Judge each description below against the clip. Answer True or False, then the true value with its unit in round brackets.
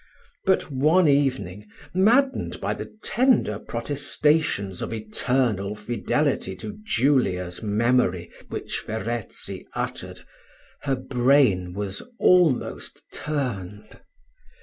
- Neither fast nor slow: False (90 wpm)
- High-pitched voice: False (125 Hz)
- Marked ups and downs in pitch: True (6.1 semitones)